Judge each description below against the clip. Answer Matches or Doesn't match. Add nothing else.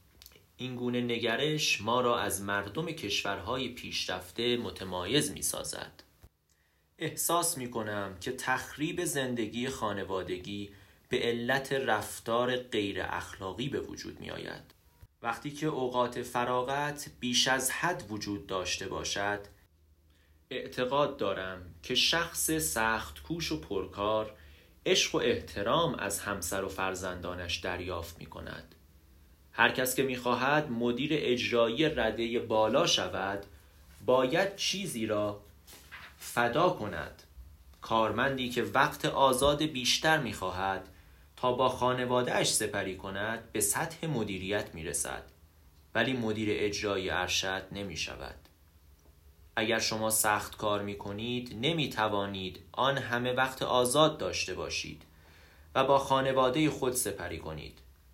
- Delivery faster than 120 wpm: Doesn't match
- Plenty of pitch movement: Matches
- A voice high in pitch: Doesn't match